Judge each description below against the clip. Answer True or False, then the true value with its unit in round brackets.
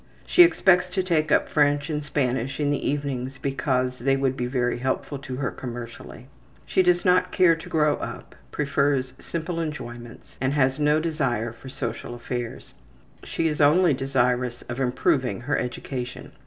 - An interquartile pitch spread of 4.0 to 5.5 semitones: False (3.4 semitones)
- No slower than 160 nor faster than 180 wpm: True (165 wpm)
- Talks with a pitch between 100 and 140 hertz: True (135 Hz)